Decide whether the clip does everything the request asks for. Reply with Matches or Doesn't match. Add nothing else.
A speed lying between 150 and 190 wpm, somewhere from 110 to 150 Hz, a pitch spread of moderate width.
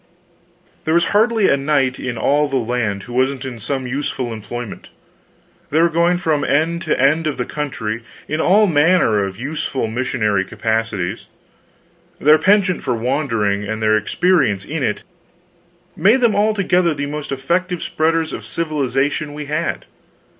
Doesn't match